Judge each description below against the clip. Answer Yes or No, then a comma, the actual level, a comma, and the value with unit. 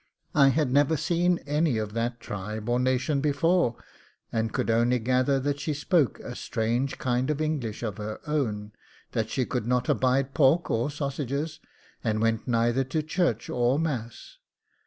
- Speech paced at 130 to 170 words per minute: Yes, average, 165 wpm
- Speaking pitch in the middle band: No, low, 130 Hz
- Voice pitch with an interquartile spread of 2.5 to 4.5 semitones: Yes, average, 4.2 semitones